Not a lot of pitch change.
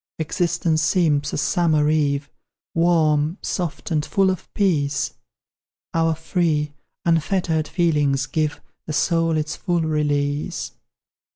Yes: narrow, 2.3 semitones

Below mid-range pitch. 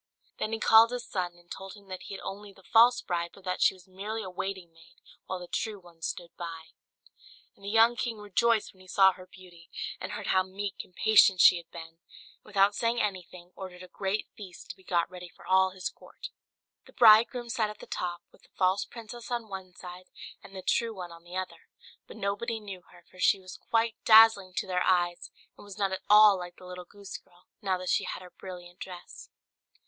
No: high, 190 Hz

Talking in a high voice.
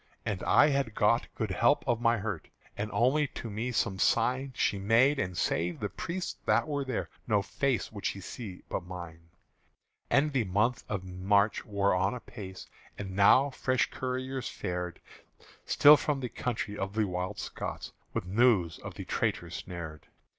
No: low, 105 Hz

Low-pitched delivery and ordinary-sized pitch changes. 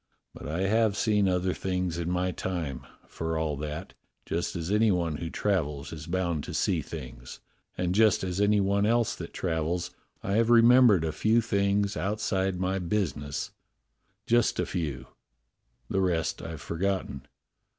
Yes: very low, 90 Hz; average, 3.8 semitones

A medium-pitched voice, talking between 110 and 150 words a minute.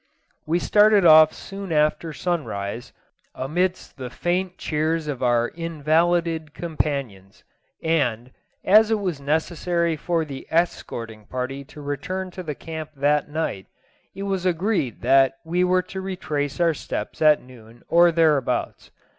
Yes: medium, 160 Hz; average, 140 wpm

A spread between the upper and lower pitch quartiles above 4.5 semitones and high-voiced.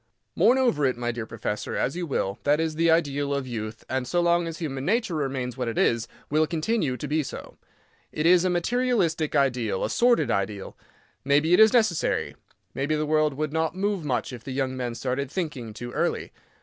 No: average, 5.0 semitones; medium, 145 Hz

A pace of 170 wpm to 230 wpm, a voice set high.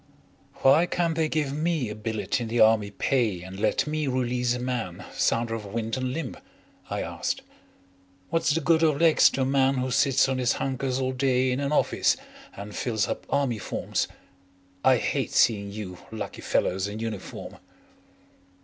No: average, 175 wpm; low, 125 Hz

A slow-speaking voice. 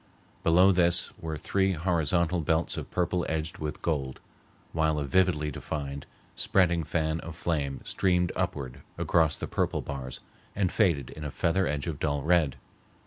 No: average, 155 wpm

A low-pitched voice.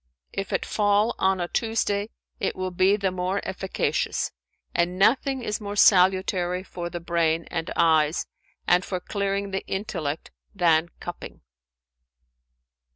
No: medium, 185 Hz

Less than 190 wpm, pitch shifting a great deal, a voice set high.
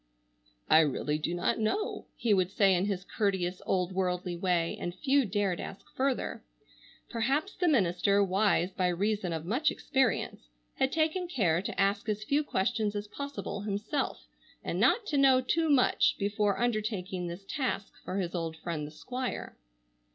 Yes: average, 165 wpm; wide, 6.0 semitones; high, 200 Hz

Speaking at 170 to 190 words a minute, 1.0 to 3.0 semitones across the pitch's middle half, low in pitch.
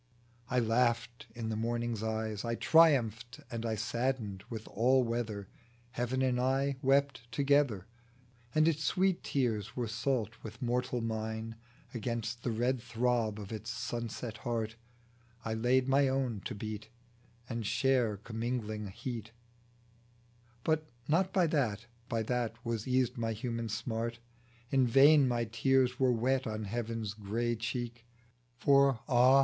No: average, 140 wpm; average, 2.7 semitones; low, 120 Hz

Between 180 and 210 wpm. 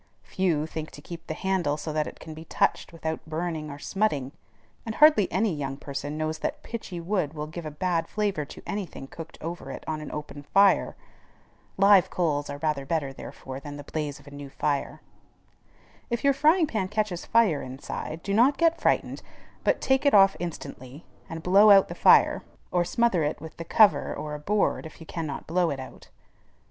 Yes: average, 200 wpm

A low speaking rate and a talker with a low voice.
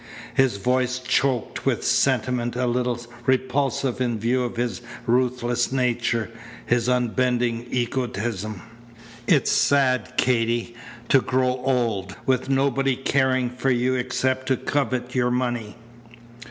Yes: slow, 125 wpm; low, 125 Hz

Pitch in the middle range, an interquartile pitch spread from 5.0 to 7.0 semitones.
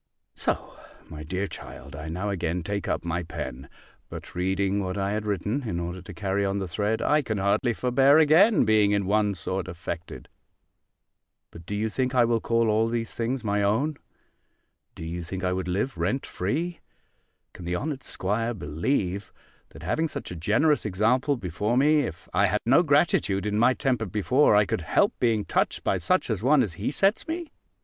No: low, 105 Hz; average, 5.3 semitones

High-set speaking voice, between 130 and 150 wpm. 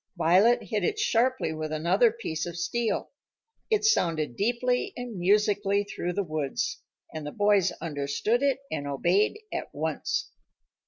Yes: high, 200 Hz; average, 145 wpm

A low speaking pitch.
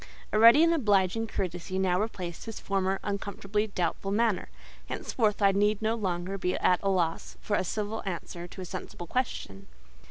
No: high, 195 Hz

